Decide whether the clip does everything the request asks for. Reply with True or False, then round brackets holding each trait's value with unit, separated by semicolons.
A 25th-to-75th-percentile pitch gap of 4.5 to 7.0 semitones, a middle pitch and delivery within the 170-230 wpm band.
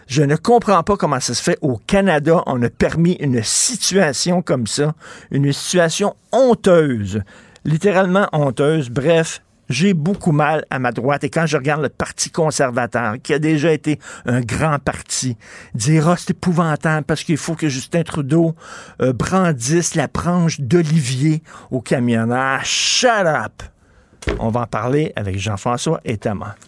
False (4.8 semitones; 150 Hz; 160 wpm)